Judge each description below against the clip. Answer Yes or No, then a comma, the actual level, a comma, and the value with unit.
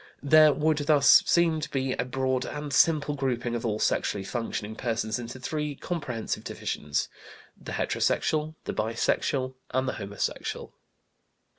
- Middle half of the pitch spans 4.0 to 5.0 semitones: Yes, average, 4.4 semitones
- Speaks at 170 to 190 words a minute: No, average, 140 wpm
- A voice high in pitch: No, low, 130 Hz